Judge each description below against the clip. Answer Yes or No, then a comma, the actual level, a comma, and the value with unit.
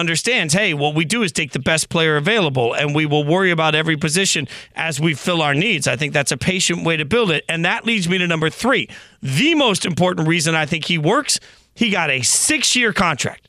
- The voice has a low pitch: No, medium, 165 Hz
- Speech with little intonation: No, average, 3.5 semitones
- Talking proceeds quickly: Yes, fast, 235 wpm